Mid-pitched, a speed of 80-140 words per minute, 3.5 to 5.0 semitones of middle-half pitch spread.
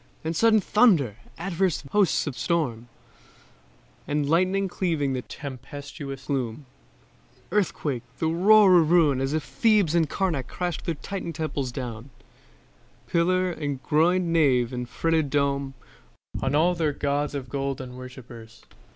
Yes: medium, 150 Hz; slow, 135 wpm; average, 4.5 semitones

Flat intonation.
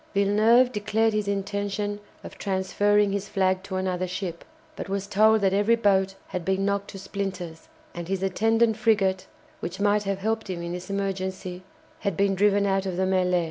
Yes: narrow, 1.5 semitones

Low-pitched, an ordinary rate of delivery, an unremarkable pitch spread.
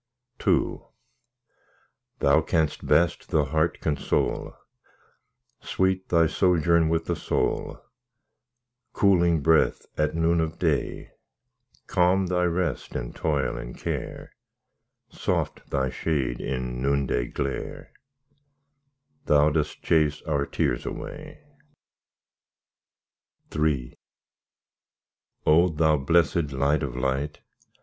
No: very low, 80 Hz; slow, 95 wpm; average, 3.2 semitones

